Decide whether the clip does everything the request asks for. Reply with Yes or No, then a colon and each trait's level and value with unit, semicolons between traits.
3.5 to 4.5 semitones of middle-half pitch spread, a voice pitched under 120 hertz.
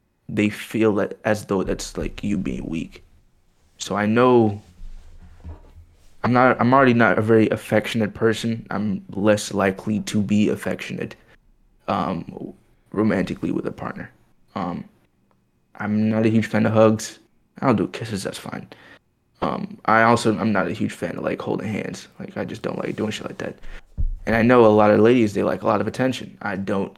No: average, 2.8 semitones; low, 105 Hz